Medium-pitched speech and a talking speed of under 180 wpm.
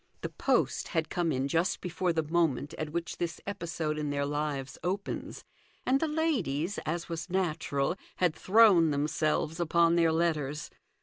Yes: medium, 165 Hz; average, 160 wpm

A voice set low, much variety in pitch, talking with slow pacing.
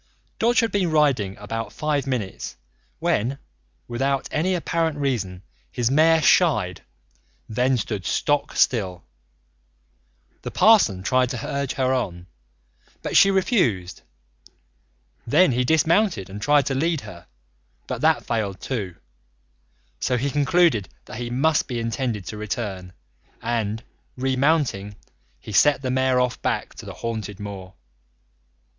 Yes: low, 125 Hz; wide, 6.0 semitones; slow, 130 wpm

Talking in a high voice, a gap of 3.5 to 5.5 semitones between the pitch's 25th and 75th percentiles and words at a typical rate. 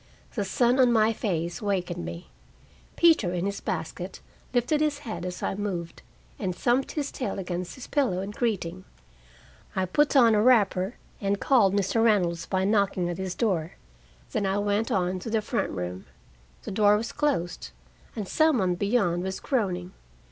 Yes: high, 200 Hz; average, 4.5 semitones; average, 170 wpm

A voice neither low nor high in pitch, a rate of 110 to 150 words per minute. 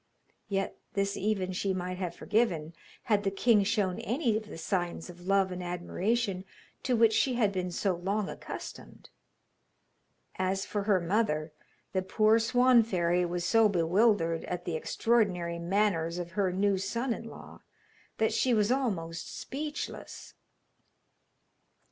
No: high, 195 Hz; average, 145 wpm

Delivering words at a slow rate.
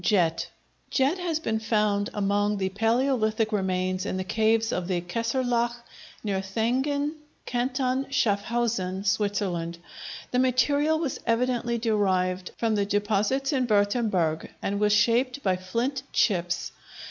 Yes: slow, 125 wpm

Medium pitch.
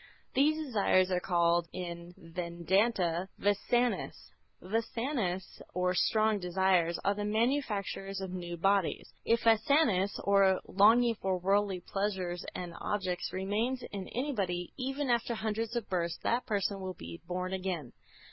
No: high, 195 Hz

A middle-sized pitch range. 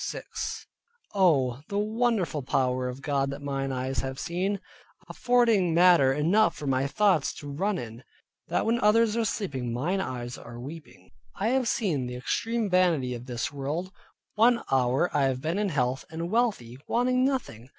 No: wide, 8.0 semitones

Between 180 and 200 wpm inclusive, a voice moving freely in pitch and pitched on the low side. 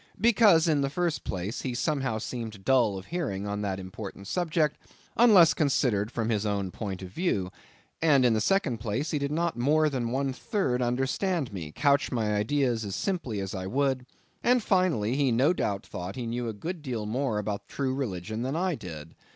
Yes: average, 195 wpm; wide, 6.6 semitones; low, 125 Hz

